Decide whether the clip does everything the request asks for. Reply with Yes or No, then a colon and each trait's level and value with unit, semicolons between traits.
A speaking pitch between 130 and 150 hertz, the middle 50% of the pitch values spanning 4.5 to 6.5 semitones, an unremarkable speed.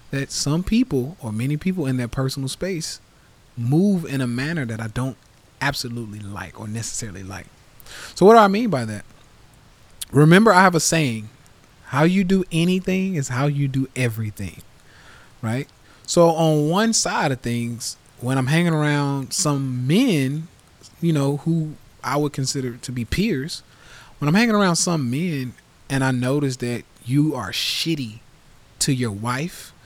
Yes: low, 135 Hz; average, 5.0 semitones; average, 165 wpm